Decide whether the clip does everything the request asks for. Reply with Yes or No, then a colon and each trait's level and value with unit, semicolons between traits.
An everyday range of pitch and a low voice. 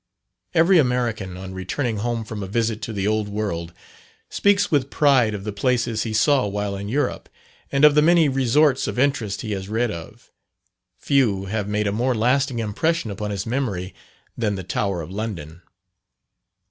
Yes: average, 4.6 semitones; low, 110 Hz